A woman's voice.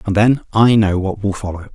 No: male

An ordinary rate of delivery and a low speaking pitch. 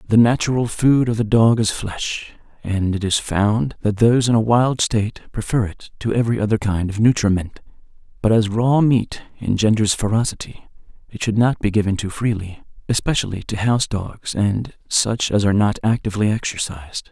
Yes: average, 175 wpm; low, 110 Hz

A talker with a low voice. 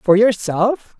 No: high, 215 Hz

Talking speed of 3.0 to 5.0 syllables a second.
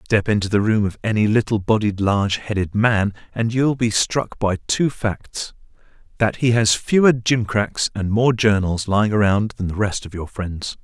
Yes: 4.7 syllables/s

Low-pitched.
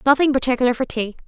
No: very high, 255 Hz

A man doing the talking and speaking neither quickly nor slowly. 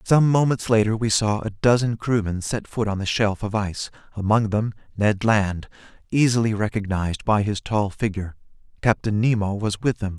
Yes: male; average, 175 wpm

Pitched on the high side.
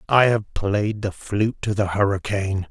No: low, 105 Hz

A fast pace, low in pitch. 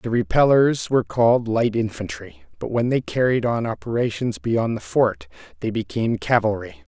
No: average, 155 wpm; low, 115 Hz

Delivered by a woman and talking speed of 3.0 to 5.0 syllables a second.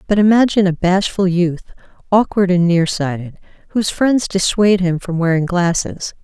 No: female; 5.2 syllables/s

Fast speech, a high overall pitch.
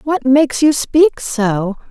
No: average, 155 wpm; very high, 265 Hz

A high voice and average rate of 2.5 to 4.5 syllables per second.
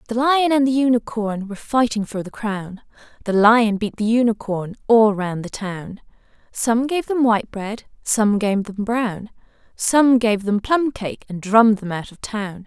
Yes: high, 220 Hz; 4.4 syllables/s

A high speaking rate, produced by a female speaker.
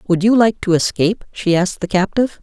Yes: fast, 225 wpm; female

